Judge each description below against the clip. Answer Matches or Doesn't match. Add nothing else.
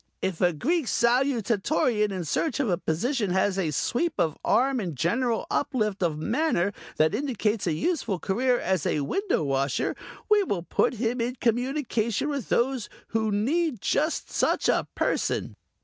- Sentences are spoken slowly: Doesn't match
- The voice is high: Matches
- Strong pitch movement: Matches